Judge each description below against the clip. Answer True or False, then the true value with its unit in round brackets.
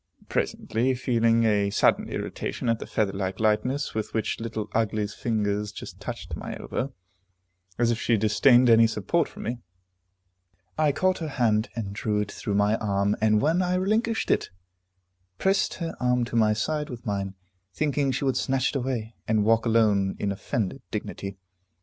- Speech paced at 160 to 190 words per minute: True (170 wpm)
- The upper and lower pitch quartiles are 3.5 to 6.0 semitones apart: True (3.8 semitones)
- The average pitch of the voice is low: True (115 Hz)